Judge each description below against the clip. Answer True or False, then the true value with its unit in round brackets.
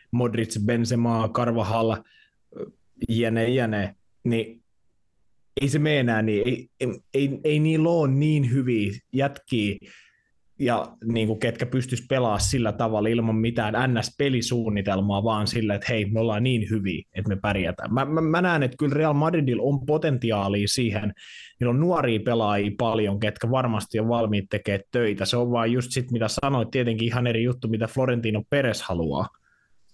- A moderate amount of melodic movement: True (3.2 semitones)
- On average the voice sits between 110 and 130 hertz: True (115 Hz)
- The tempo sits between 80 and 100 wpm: False (155 wpm)